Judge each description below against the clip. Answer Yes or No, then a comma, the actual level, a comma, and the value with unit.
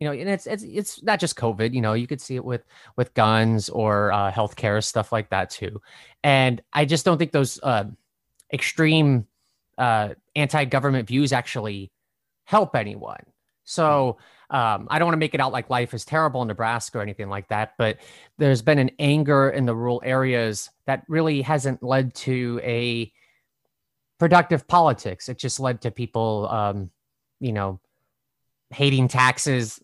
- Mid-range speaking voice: No, low, 125 Hz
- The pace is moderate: Yes, average, 170 wpm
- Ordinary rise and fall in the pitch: Yes, average, 4.3 semitones